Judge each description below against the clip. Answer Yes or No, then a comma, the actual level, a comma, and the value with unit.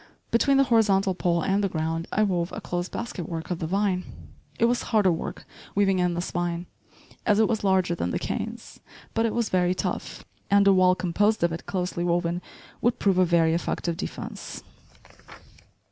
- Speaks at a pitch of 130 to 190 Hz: Yes, medium, 185 Hz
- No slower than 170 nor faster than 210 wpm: Yes, average, 185 wpm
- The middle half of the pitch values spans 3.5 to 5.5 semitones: No, average, 3.1 semitones